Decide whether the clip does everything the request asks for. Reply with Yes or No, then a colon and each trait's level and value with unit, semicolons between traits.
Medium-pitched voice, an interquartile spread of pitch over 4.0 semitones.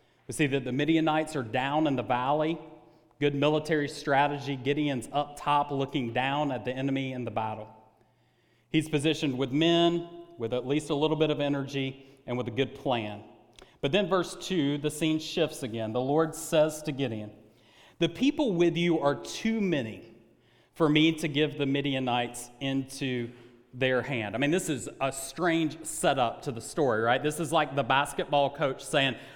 No: medium, 145 Hz; average, 3.7 semitones